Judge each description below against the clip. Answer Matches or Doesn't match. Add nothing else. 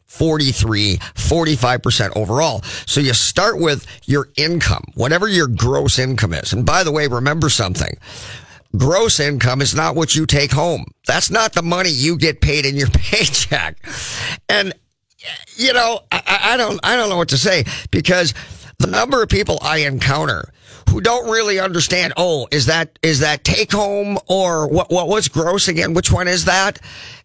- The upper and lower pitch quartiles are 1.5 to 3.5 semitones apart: Doesn't match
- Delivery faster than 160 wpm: Matches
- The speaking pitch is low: Doesn't match